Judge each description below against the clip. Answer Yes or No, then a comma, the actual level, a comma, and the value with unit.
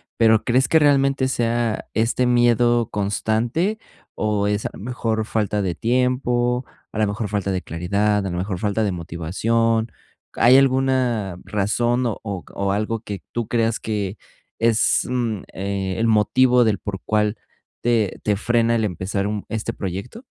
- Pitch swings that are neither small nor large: Yes, average, 3.0 semitones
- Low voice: Yes, low, 110 Hz